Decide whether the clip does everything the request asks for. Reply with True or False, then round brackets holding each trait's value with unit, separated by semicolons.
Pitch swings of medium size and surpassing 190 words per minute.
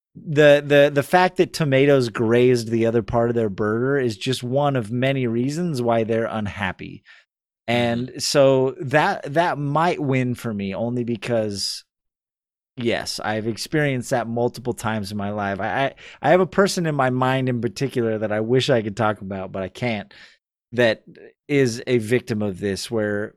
False (3.8 semitones; 175 wpm)